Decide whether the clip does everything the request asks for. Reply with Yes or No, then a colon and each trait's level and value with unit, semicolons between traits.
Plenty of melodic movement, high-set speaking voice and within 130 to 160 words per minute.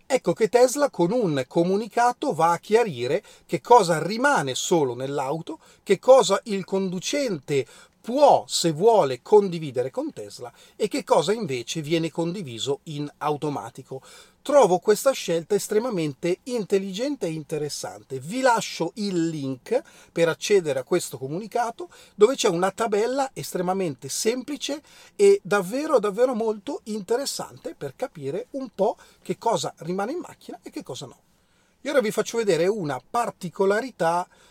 Yes: wide, 6.7 semitones; high, 200 Hz; average, 135 wpm